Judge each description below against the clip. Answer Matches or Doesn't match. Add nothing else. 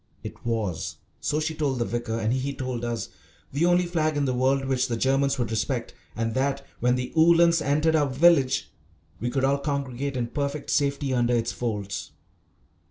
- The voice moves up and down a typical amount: Matches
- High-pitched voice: Doesn't match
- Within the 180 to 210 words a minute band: Matches